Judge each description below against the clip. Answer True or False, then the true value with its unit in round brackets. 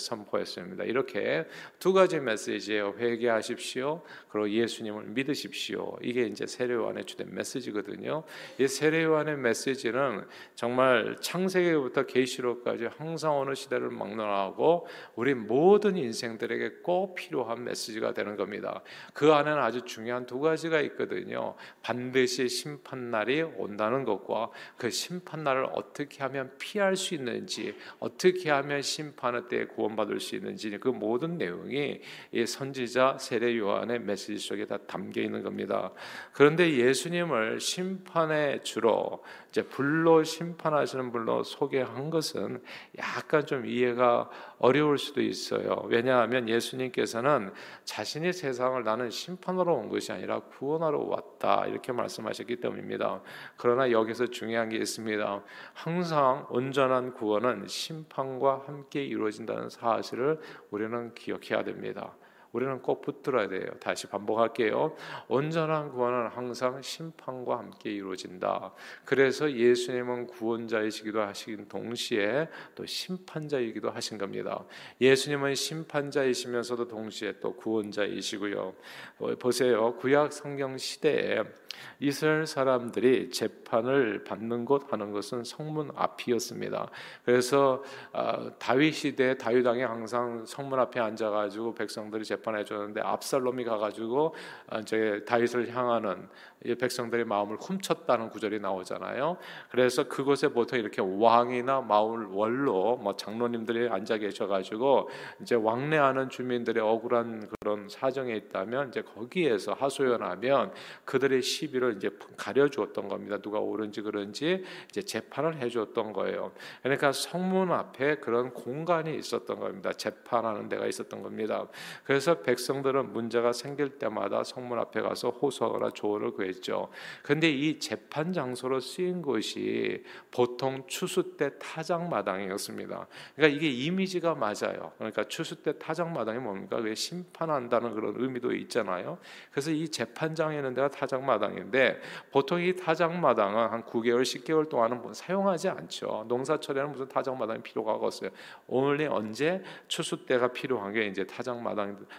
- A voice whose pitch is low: True (130 Hz)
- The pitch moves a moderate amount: True (4.5 semitones)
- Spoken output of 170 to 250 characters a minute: False (330 characters per minute)